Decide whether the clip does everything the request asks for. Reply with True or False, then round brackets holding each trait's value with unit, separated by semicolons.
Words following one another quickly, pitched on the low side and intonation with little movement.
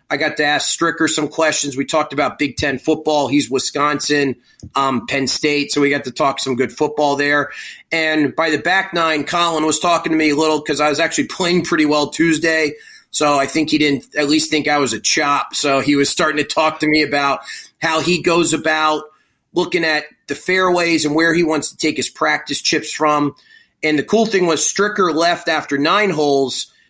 False (215 wpm; 155 Hz; 2.0 semitones)